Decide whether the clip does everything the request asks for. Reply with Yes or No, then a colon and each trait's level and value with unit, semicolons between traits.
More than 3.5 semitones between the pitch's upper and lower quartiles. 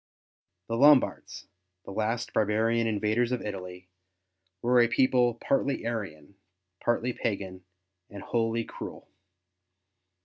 No: average, 2.9 semitones